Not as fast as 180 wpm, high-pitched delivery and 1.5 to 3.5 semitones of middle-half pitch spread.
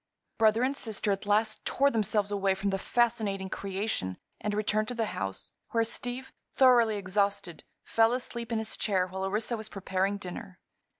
Yes: average, 170 wpm; high, 210 Hz; average, 2.7 semitones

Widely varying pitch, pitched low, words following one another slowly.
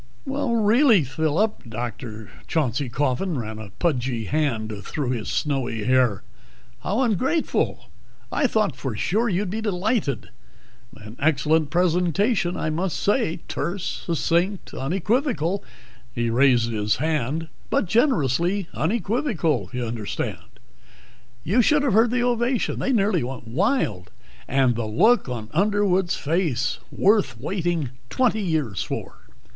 No: wide, 8.7 semitones; medium, 160 Hz; slow, 125 wpm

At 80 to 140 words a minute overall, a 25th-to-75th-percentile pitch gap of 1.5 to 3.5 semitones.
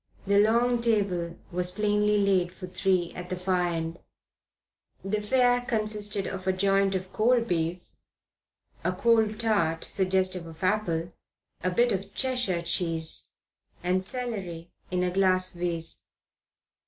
Yes: slow, 135 wpm; average, 3.1 semitones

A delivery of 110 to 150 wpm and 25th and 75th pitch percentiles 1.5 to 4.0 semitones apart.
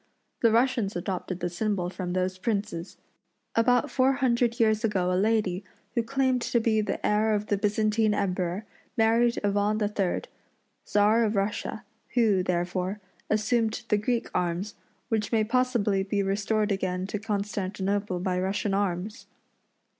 Yes: average, 145 wpm; average, 2.8 semitones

